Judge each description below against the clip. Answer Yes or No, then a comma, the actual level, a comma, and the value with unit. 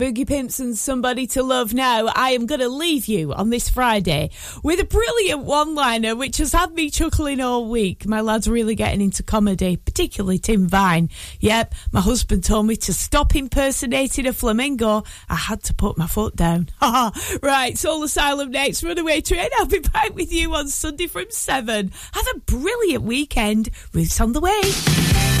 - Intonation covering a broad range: Yes, wide, 6.0 semitones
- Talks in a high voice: Yes, very high, 255 Hz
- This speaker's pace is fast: No, average, 185 wpm